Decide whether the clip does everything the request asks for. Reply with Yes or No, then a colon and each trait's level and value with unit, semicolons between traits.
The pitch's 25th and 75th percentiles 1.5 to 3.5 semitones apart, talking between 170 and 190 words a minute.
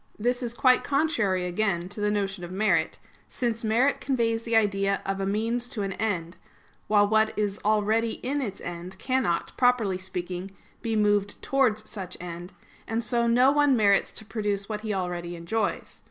Yes: average, 3.2 semitones; average, 175 wpm